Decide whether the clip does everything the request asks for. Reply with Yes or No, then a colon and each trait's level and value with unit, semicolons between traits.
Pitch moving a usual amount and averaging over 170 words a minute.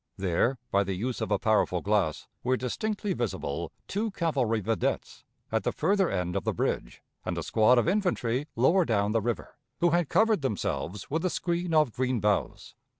No: wide, 8.6 semitones; average, 185 wpm